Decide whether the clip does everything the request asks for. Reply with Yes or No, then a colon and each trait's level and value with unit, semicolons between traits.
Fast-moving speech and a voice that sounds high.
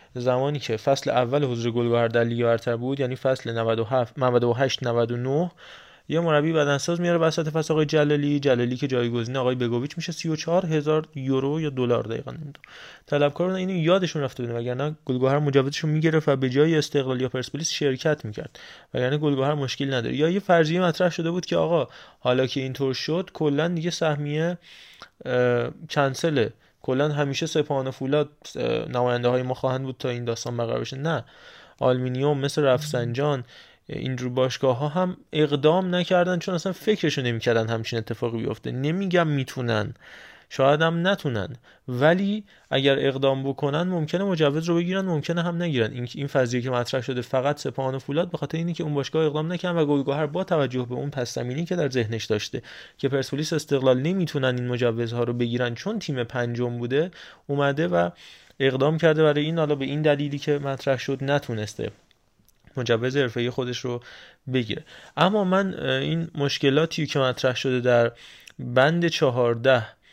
No: fast, 165 wpm; medium, 140 Hz